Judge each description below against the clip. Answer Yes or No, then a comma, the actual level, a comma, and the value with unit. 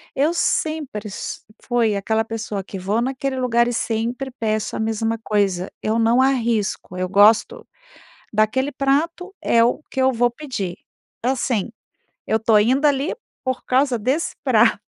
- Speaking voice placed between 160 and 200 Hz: No, high, 235 Hz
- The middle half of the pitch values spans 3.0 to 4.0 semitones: Yes, average, 3.6 semitones